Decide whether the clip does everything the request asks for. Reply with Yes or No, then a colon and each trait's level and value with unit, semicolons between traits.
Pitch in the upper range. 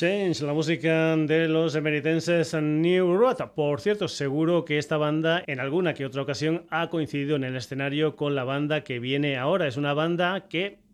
No: medium, 155 Hz